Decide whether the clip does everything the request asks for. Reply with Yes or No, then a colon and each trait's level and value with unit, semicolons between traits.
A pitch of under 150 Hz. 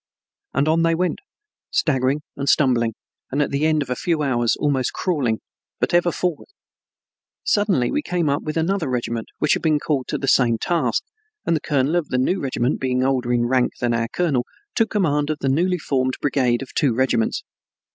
Yes: medium, 140 Hz